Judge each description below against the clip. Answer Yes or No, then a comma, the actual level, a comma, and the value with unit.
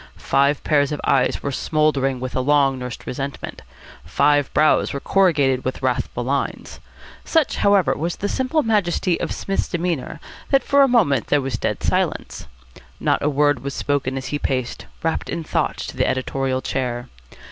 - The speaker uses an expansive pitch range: No, average, 4.3 semitones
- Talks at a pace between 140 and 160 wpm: No, average, 170 wpm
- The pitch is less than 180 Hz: Yes, medium, 140 Hz